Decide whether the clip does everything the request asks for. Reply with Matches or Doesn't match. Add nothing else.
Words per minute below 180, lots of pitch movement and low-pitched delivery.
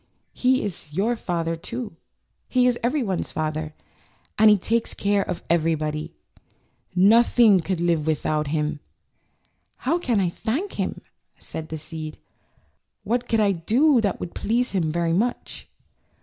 Doesn't match